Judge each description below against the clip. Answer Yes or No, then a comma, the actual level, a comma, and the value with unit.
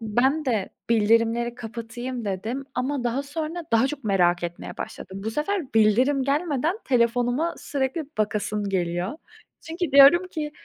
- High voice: Yes, high, 245 Hz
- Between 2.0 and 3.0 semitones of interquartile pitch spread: No, average, 4.7 semitones